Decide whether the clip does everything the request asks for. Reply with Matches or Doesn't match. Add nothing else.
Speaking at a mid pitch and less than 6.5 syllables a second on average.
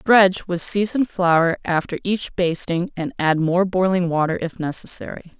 Matches